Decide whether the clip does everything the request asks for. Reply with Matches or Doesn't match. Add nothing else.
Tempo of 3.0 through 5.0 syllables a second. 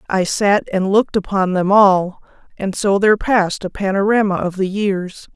Matches